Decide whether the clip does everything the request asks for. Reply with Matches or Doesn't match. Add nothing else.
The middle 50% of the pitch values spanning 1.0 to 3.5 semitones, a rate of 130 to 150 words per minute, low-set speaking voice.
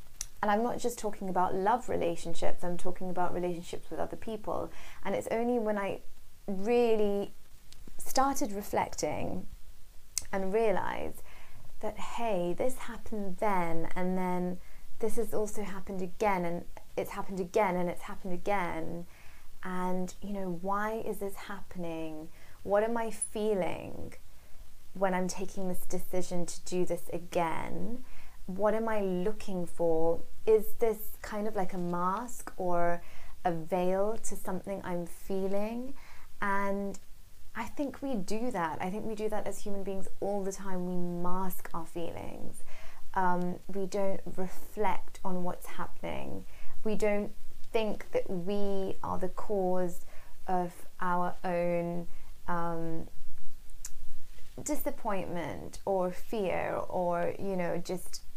Doesn't match